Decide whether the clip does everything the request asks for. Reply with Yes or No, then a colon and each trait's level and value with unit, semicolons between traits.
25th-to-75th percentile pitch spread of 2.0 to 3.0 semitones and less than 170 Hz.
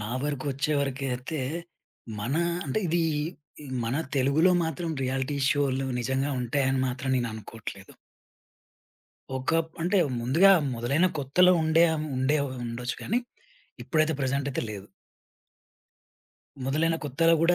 No: average, 3.7 semitones; low, 135 Hz